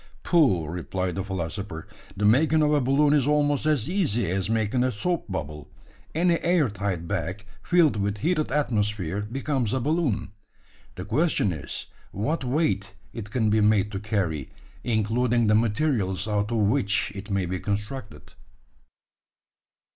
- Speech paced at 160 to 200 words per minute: No, average, 150 wpm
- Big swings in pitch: Yes, wide, 6.0 semitones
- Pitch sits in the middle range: No, low, 110 Hz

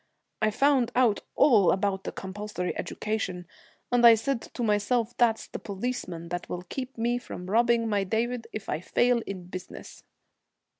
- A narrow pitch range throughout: No, average, 4.0 semitones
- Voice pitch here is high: Yes, high, 220 Hz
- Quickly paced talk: No, average, 160 wpm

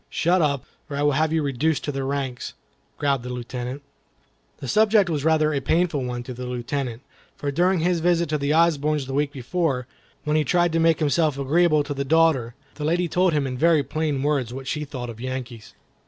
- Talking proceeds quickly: Yes, fast, 215 wpm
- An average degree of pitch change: Yes, average, 3.4 semitones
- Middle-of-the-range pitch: Yes, medium, 145 Hz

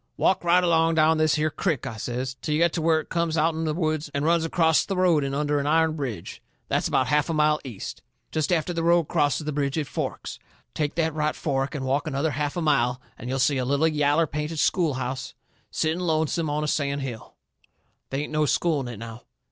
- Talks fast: Yes, fast, 235 wpm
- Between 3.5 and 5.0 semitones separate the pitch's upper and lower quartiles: No, narrow, 2.6 semitones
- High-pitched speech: No, medium, 150 Hz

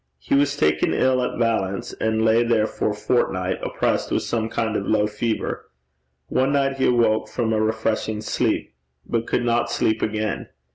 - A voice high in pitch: No, low, 110 Hz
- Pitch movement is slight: Yes, narrow, 1.8 semitones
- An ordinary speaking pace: Yes, average, 180 wpm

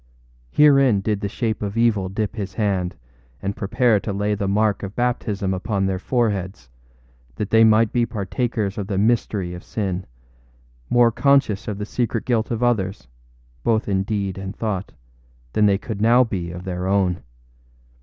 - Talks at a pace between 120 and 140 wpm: No, average, 170 wpm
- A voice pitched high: No, low, 105 Hz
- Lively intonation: No, average, 2.8 semitones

